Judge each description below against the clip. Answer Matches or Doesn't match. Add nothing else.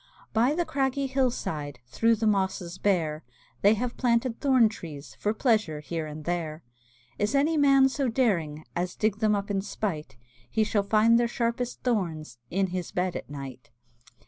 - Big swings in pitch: Matches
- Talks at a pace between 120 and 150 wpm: Doesn't match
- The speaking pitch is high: Matches